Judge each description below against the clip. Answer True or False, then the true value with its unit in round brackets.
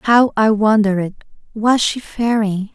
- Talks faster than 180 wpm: False (130 wpm)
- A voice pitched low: False (215 Hz)